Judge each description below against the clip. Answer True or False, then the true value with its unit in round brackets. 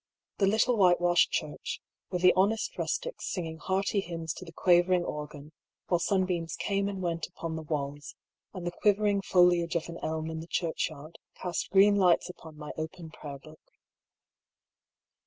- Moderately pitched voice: True (175 Hz)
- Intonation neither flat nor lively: True (3.0 semitones)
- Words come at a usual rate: True (160 wpm)